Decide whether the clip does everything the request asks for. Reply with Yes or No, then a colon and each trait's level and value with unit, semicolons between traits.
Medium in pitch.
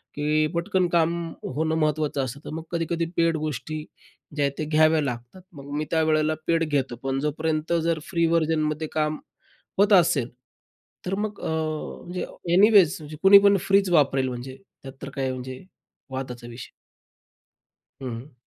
Yes: medium, 155 Hz